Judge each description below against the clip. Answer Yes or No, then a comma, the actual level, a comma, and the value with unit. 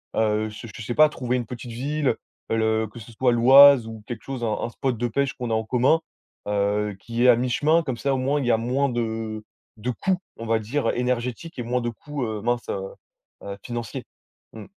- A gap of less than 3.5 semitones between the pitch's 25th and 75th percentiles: Yes, average, 2.8 semitones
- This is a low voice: Yes, low, 120 Hz